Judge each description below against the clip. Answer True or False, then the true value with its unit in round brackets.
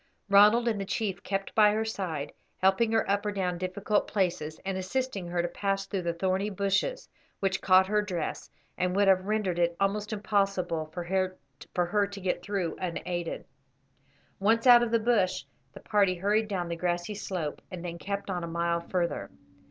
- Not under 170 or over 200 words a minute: True (185 wpm)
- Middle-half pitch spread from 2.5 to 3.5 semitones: True (2.8 semitones)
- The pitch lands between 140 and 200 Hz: True (190 Hz)